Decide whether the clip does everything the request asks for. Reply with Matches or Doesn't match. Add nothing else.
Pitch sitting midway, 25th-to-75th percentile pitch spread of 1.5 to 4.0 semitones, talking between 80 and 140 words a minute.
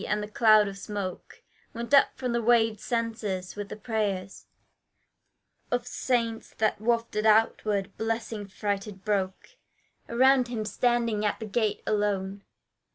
Doesn't match